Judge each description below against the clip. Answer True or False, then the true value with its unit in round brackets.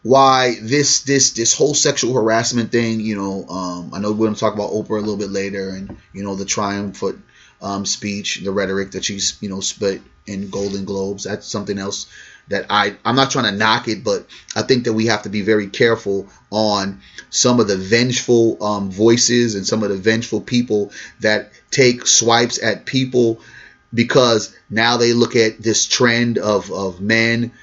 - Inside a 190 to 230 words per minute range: True (195 wpm)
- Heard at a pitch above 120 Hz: False (110 Hz)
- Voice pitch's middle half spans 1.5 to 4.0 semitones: True (2.9 semitones)